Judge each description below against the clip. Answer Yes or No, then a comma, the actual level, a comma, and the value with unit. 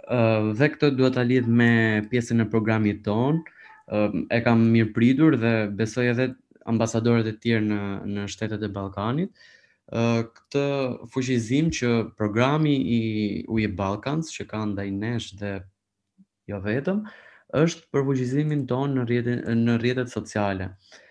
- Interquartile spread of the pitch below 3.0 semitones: No, average, 3.5 semitones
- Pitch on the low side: Yes, low, 115 Hz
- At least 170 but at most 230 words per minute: No, average, 140 wpm